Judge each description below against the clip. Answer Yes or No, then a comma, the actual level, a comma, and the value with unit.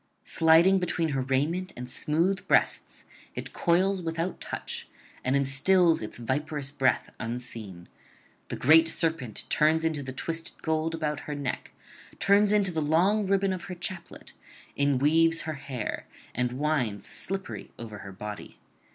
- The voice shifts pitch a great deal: No, average, 4.6 semitones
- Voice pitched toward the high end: No, medium, 155 Hz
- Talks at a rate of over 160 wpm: No, average, 145 wpm